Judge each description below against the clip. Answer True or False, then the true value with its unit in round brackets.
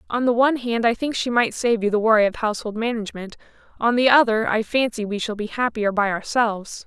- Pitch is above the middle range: True (225 Hz)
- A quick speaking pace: True (225 wpm)